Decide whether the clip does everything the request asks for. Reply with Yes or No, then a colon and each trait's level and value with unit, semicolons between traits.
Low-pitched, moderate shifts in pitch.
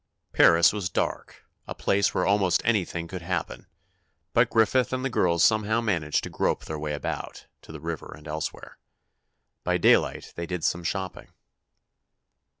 Yes: very low, 90 Hz; average, 4.0 semitones